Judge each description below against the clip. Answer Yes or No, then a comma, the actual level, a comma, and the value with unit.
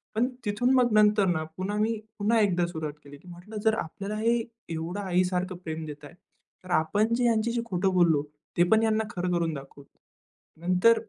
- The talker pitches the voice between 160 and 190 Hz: Yes, medium, 185 Hz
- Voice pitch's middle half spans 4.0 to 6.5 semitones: Yes, average, 4.3 semitones